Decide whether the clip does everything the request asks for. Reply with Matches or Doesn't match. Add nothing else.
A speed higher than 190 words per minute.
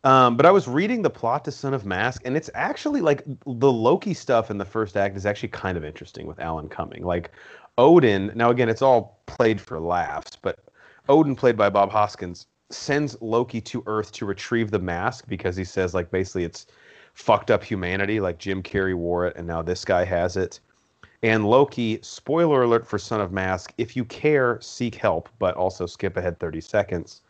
Matches